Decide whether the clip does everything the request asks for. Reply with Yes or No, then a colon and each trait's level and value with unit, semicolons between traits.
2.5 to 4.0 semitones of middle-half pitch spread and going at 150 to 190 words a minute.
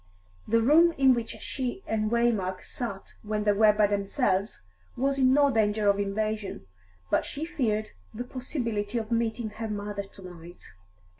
Yes: average, 3.2 semitones; average, 160 wpm